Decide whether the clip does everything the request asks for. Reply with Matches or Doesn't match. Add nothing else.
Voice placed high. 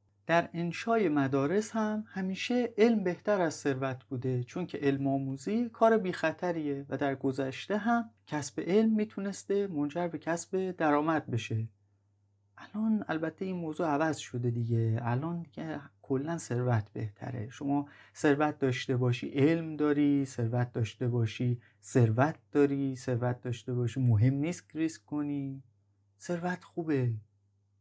Doesn't match